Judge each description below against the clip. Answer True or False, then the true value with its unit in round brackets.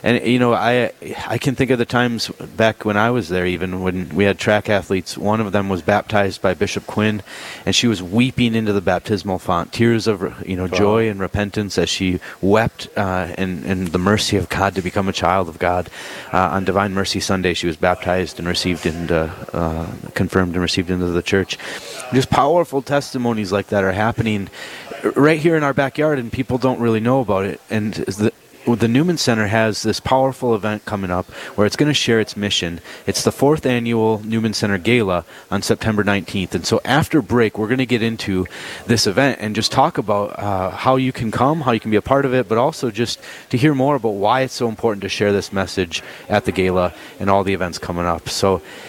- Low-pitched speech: True (105 Hz)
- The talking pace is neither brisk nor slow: False (220 wpm)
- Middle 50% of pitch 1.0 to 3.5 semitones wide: False (4.2 semitones)